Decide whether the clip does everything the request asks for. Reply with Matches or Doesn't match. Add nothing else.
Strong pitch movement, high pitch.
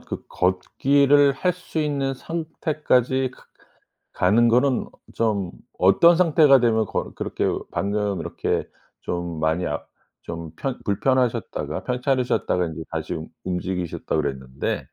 Doesn't match